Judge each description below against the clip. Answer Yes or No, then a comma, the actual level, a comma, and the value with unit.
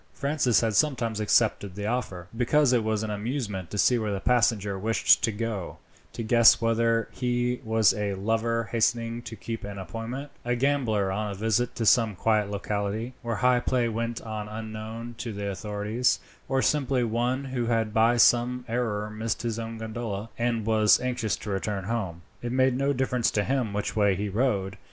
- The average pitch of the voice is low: Yes, low, 115 Hz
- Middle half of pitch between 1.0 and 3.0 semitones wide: Yes, narrow, 2.6 semitones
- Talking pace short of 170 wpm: No, average, 185 wpm